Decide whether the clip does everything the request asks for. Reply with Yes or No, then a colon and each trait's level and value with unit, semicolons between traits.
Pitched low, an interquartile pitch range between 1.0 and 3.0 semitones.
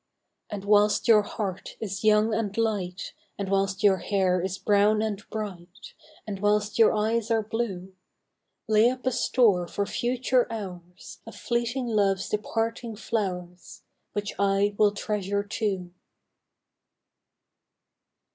No: high, 205 Hz; narrow, 2.4 semitones